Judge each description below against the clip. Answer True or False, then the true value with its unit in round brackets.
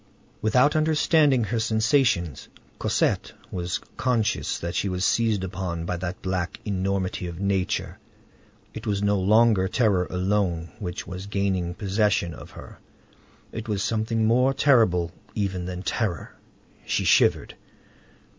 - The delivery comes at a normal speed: False (130 wpm)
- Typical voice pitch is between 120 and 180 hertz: False (100 Hz)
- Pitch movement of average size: True (3.6 semitones)